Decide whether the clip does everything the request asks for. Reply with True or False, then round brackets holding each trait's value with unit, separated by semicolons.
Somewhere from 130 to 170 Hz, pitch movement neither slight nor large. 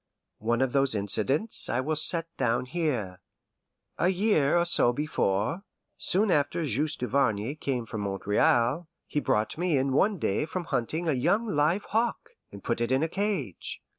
False (140 Hz; 6.3 semitones)